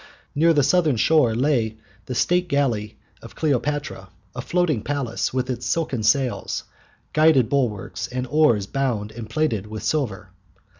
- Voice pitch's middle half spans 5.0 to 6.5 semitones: Yes, wide, 5.4 semitones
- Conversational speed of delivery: Yes, average, 145 wpm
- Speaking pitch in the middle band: No, low, 130 Hz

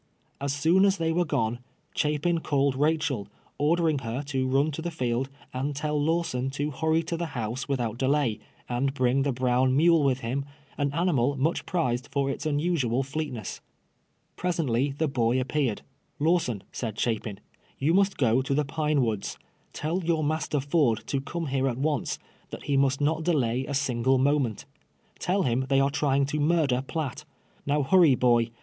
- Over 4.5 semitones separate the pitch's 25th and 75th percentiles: No, average, 3.5 semitones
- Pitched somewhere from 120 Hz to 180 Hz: Yes, medium, 140 Hz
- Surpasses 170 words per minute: Yes, average, 180 wpm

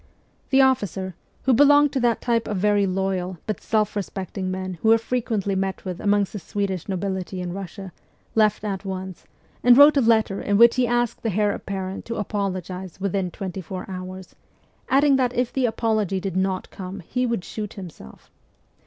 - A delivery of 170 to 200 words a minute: Yes, average, 180 wpm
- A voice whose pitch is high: Yes, high, 200 Hz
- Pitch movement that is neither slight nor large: Yes, average, 3.5 semitones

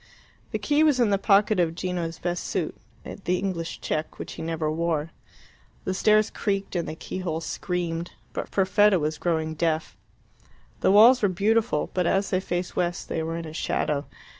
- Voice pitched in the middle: Yes, medium, 175 Hz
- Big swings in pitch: No, average, 3.2 semitones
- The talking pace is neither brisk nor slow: Yes, average, 180 wpm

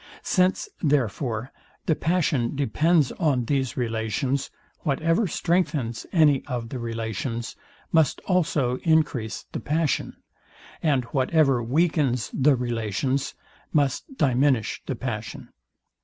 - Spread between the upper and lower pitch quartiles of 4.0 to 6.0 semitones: Yes, average, 4.8 semitones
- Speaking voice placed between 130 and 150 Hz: Yes, low, 135 Hz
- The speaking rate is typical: No, slow, 105 wpm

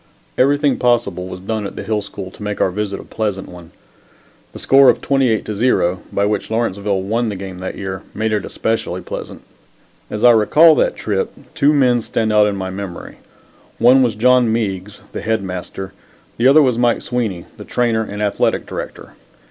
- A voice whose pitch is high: No, low, 110 Hz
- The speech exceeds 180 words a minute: Yes, average, 190 wpm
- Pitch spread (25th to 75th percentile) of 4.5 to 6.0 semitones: No, average, 3.7 semitones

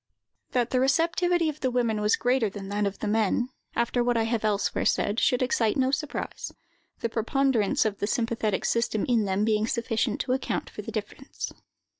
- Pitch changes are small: No, average, 3.3 semitones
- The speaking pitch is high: Yes, high, 230 Hz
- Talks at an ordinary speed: Yes, average, 190 wpm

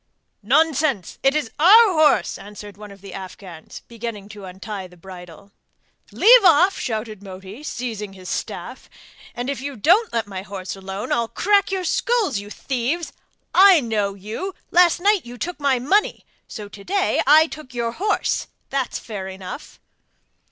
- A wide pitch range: Yes, wide, 8.3 semitones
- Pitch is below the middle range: No, high, 235 Hz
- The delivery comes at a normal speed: Yes, average, 160 wpm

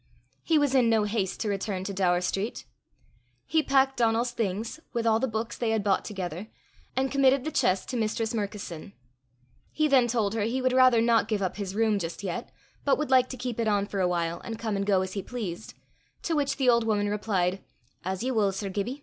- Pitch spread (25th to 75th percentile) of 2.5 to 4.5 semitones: Yes, average, 3.9 semitones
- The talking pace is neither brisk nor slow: No, fast, 225 wpm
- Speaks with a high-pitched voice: Yes, high, 220 Hz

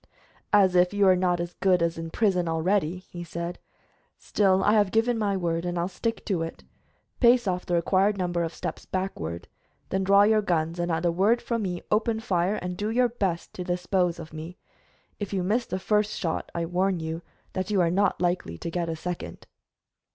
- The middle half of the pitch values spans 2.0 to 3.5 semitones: Yes, average, 2.9 semitones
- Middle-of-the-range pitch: Yes, medium, 180 Hz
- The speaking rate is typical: No, fast, 210 wpm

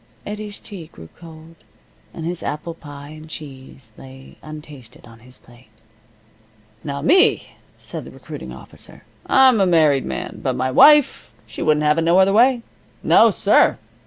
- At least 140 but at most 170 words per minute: Yes, average, 160 wpm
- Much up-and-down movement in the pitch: Yes, wide, 6.0 semitones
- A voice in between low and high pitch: Yes, medium, 155 Hz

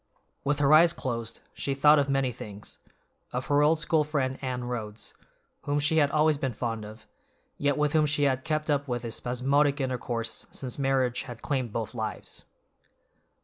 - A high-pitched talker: No, low, 135 Hz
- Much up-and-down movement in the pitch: No, average, 3.2 semitones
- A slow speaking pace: No, average, 180 wpm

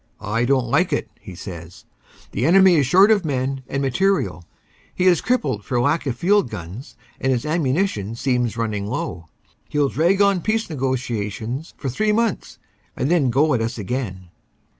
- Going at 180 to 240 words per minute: Yes, average, 185 wpm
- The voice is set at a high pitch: No, low, 135 Hz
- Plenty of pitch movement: Yes, wide, 7.3 semitones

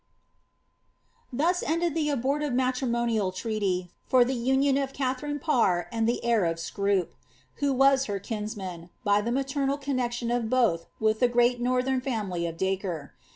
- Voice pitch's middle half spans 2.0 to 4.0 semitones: No, average, 4.8 semitones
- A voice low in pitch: No, high, 240 Hz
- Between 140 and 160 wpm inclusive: Yes, average, 155 wpm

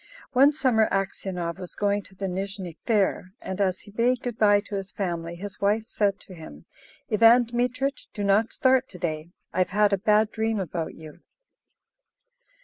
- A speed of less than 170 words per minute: No, average, 180 wpm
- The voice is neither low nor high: No, high, 200 Hz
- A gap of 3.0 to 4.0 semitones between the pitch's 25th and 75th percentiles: Yes, average, 3.3 semitones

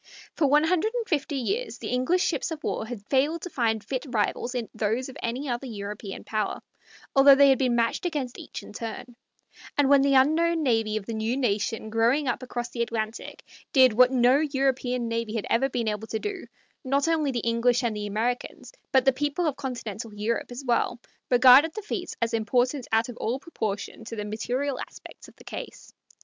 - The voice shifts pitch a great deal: No, average, 3.6 semitones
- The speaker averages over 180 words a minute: Yes, average, 200 wpm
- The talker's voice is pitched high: Yes, very high, 250 Hz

